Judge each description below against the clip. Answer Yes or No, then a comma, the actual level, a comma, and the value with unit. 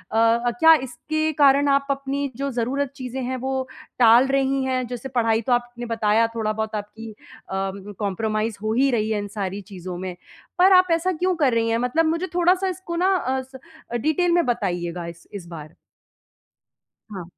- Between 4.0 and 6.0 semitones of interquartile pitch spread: Yes, average, 4.4 semitones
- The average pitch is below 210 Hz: No, high, 245 Hz